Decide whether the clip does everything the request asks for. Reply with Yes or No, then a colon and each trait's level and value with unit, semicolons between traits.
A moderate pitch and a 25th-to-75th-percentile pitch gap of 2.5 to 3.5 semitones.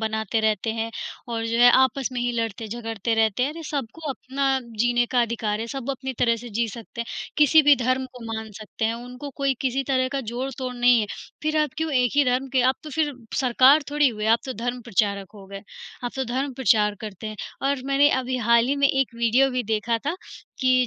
No: high, 245 Hz; average, 3.0 semitones